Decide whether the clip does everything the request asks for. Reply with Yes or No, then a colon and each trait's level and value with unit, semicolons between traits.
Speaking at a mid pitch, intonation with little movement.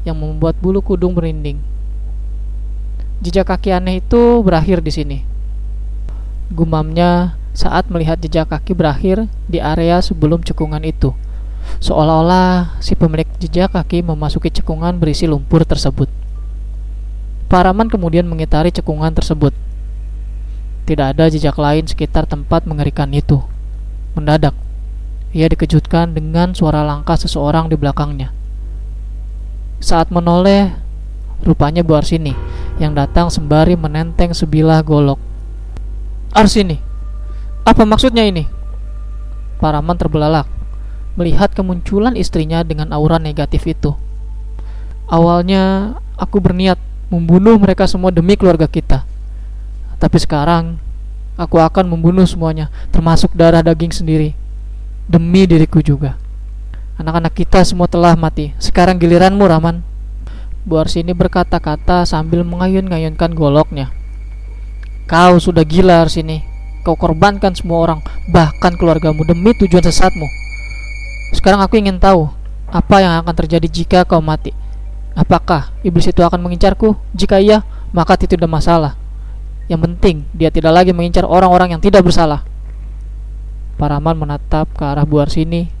No: medium, 165 Hz; average, 3.3 semitones